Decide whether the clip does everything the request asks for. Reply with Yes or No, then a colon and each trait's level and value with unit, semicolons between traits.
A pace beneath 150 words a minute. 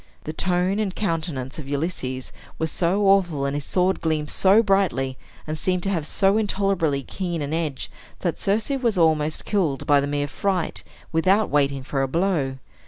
No: average, 175 wpm